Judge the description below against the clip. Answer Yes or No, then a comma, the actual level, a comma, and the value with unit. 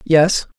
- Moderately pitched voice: Yes, medium, 165 Hz